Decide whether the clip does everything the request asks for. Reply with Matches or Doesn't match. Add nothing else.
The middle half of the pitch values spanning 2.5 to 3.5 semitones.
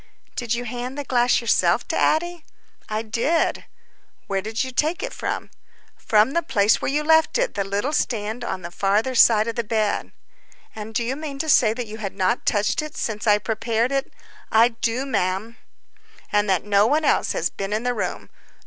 Doesn't match